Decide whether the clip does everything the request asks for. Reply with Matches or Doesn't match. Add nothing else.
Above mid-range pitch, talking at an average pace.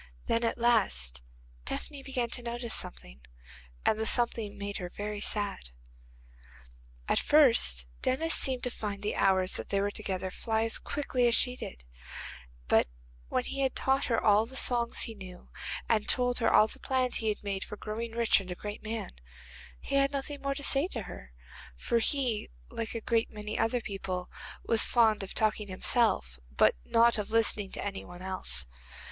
Matches